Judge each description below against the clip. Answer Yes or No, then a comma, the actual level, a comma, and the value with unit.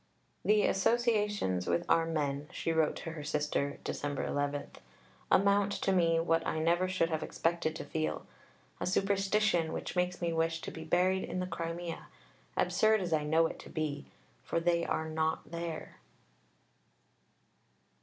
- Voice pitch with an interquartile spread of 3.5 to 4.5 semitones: No, average, 2.7 semitones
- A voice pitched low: No, medium, 165 Hz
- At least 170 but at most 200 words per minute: No, average, 160 wpm